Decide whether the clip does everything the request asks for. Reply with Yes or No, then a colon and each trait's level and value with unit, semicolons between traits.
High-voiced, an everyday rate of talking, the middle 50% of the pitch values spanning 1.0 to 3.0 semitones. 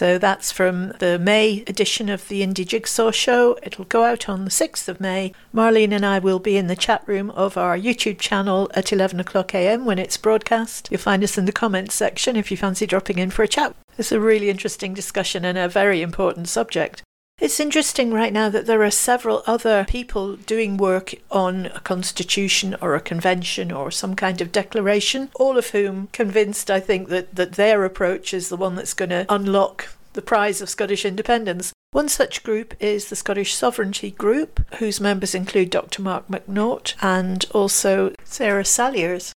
Yes: high, 200 Hz; average, 195 wpm; narrow, 2.4 semitones